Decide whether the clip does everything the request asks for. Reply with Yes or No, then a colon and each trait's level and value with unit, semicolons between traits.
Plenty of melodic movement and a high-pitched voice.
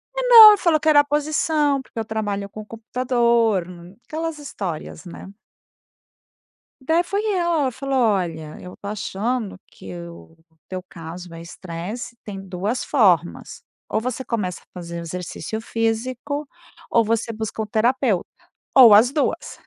Yes: wide, 6.4 semitones; high, 225 Hz